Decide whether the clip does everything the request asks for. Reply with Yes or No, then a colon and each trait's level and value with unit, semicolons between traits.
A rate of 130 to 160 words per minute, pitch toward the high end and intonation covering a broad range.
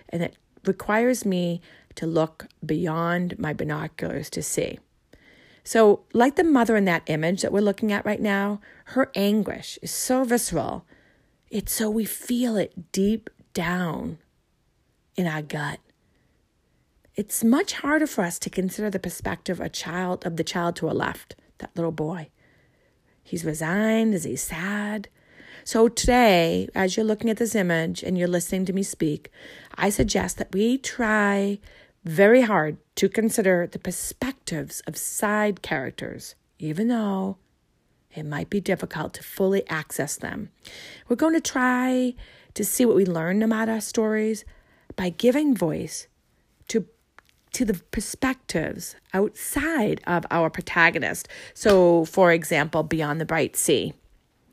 No: average, 145 wpm; high, 200 Hz; average, 4.5 semitones